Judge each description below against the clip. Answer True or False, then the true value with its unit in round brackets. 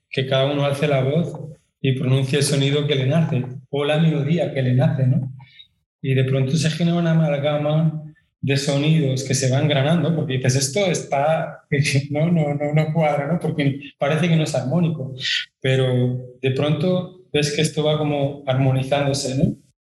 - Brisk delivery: False (180 wpm)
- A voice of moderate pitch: True (145 Hz)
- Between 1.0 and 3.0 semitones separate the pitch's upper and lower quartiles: True (2.6 semitones)